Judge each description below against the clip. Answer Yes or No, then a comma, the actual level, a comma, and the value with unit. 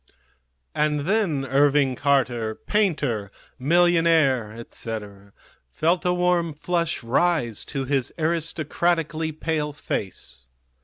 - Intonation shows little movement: No, average, 5.3 semitones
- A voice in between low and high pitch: Yes, medium, 150 Hz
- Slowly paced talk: Yes, slow, 95 wpm